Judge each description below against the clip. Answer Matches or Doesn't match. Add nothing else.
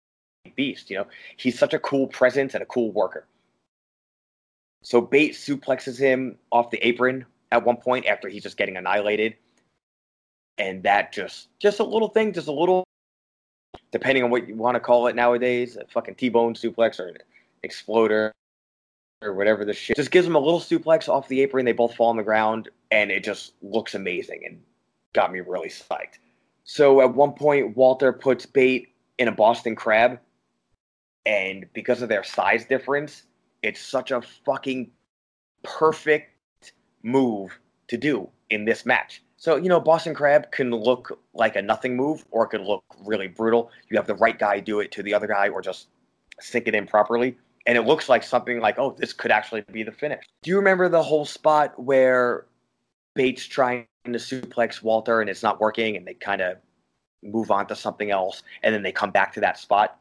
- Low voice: Matches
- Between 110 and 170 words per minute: Doesn't match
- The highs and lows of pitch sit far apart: Doesn't match